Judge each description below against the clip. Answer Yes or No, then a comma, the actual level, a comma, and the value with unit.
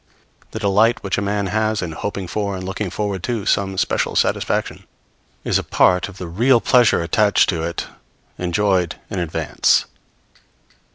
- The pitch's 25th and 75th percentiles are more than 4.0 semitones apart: No, average, 2.8 semitones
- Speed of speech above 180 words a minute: No, average, 160 wpm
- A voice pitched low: Yes, low, 100 Hz